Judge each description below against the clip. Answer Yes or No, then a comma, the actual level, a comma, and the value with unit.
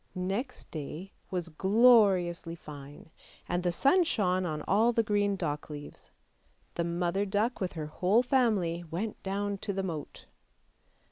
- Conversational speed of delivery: Yes, average, 145 wpm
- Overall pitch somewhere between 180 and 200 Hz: Yes, medium, 185 Hz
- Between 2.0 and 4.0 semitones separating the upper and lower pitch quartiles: Yes, average, 3.5 semitones